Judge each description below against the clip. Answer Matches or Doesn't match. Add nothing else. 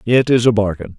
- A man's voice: Matches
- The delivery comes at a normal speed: Doesn't match